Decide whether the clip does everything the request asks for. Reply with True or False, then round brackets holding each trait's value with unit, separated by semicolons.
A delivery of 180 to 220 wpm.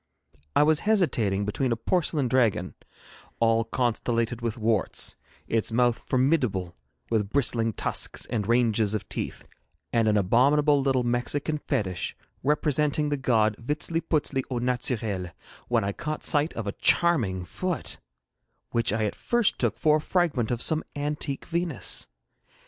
False (140 wpm)